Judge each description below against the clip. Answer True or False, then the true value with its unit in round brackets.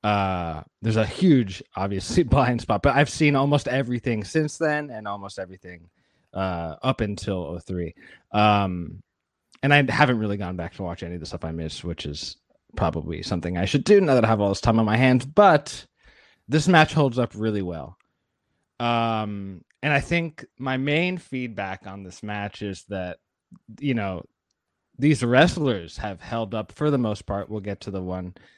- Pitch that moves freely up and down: True (6.1 semitones)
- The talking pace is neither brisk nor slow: True (185 wpm)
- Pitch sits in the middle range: False (105 Hz)